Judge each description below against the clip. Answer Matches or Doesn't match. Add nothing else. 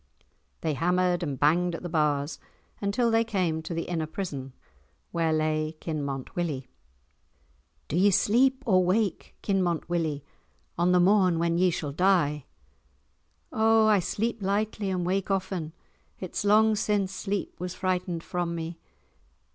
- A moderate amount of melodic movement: Matches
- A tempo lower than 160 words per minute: Matches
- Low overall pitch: Doesn't match